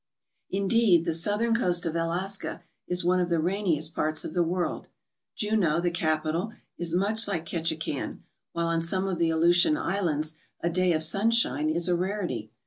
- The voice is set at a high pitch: No, medium, 175 Hz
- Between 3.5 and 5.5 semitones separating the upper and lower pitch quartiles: No, average, 3.1 semitones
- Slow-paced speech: No, average, 170 wpm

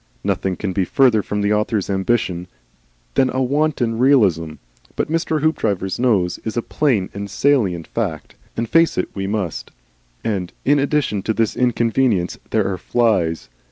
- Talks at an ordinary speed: Yes, average, 160 wpm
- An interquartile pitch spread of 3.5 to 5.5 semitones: Yes, average, 5.2 semitones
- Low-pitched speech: Yes, low, 110 Hz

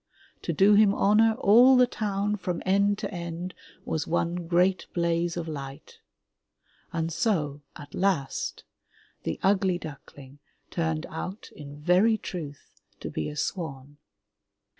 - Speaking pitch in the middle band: Yes, medium, 175 Hz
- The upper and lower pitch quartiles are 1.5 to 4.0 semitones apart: No, average, 4.4 semitones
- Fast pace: No, slow, 135 wpm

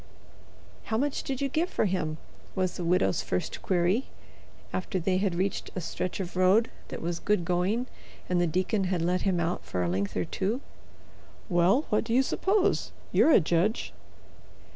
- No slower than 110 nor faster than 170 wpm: No, average, 180 wpm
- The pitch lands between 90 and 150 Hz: No, medium, 185 Hz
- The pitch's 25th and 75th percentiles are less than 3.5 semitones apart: No, average, 4.0 semitones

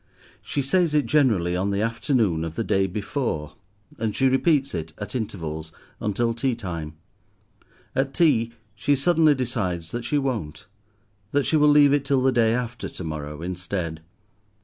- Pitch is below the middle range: Yes, low, 115 Hz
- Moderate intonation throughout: No, wide, 7.5 semitones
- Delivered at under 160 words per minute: No, average, 165 wpm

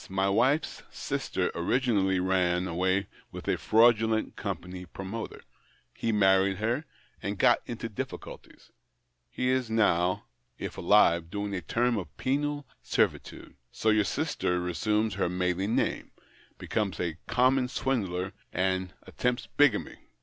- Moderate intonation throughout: Yes, average, 4.1 semitones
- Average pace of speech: No, slow, 130 wpm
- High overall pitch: No, low, 100 Hz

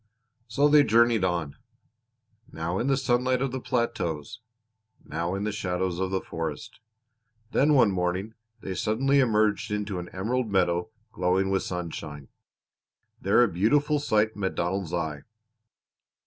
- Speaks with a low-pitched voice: Yes, low, 100 Hz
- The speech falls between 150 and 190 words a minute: No, average, 140 wpm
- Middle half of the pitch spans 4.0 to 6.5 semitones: Yes, average, 5.1 semitones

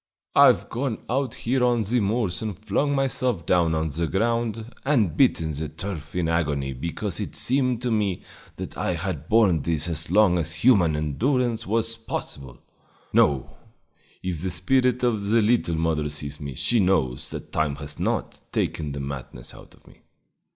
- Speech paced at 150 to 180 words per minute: Yes, average, 170 wpm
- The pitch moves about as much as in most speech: No, wide, 6.9 semitones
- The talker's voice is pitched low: Yes, very low, 95 Hz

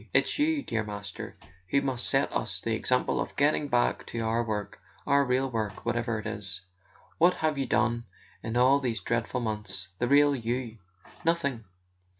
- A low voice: Yes, low, 120 Hz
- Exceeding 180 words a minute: No, average, 165 wpm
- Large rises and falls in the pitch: No, average, 4.0 semitones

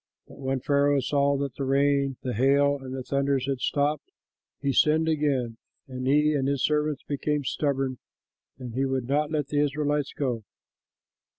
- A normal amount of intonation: No, narrow, 1.7 semitones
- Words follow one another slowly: No, average, 175 wpm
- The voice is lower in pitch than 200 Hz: Yes, medium, 140 Hz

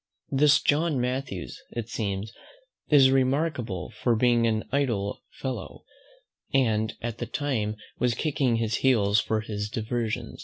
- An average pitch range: Yes, average, 3.7 semitones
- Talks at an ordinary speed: No, slow, 130 wpm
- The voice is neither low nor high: No, low, 120 Hz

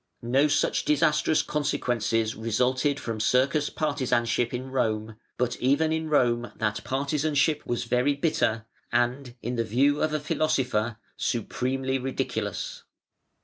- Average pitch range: Yes, average, 3.7 semitones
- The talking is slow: Yes, slow, 125 wpm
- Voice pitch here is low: Yes, low, 130 Hz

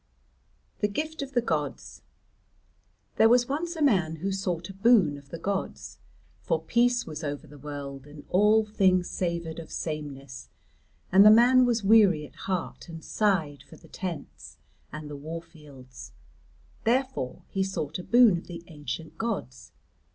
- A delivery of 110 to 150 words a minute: No, average, 160 wpm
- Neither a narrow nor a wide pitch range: No, wide, 6.5 semitones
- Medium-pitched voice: Yes, medium, 175 Hz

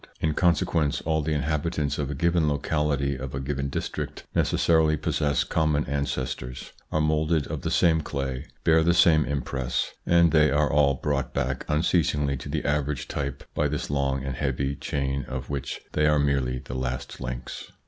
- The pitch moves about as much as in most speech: No, narrow, 2.2 semitones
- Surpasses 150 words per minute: Yes, average, 175 wpm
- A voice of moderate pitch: No, very low, 70 Hz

